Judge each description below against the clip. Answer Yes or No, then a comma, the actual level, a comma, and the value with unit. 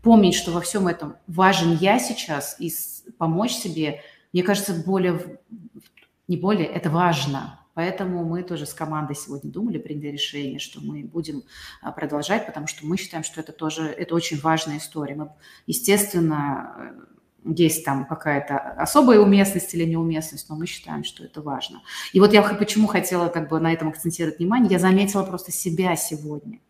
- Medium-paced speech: No, fast, 165 wpm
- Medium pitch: Yes, medium, 170 Hz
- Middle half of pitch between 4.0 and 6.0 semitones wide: No, average, 3.6 semitones